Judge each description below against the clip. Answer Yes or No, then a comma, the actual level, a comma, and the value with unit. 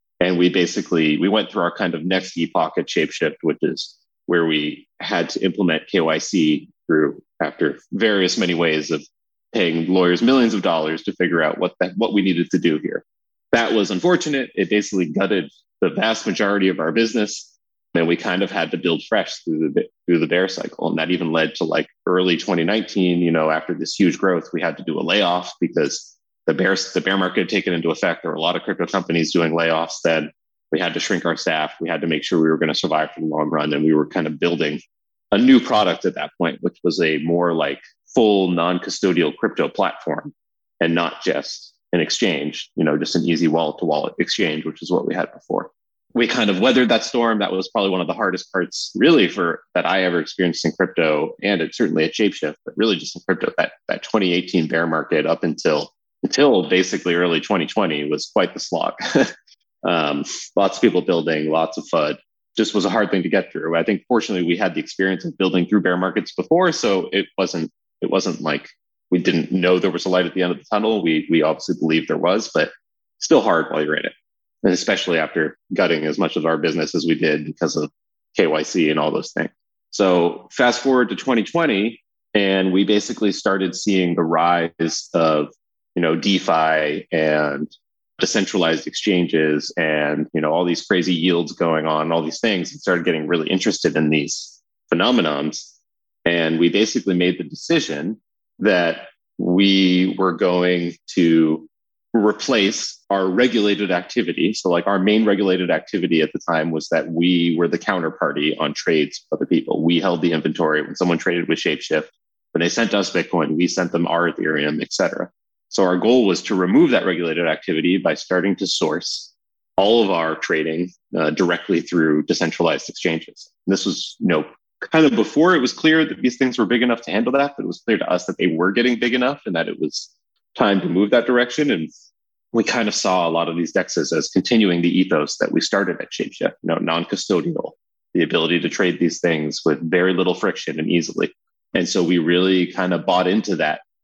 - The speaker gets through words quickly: Yes, fast, 210 wpm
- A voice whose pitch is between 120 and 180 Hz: No, very low, 90 Hz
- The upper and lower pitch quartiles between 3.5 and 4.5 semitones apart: No, average, 3.1 semitones